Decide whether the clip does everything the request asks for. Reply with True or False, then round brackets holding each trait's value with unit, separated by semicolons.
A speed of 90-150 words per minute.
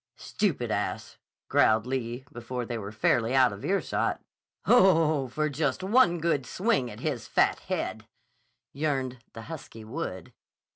True (140 wpm)